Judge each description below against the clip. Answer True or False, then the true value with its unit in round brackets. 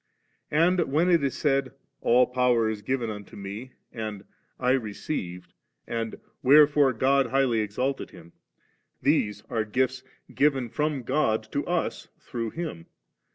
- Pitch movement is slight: False (4.1 semitones)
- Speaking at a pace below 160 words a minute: True (140 wpm)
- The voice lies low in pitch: True (125 Hz)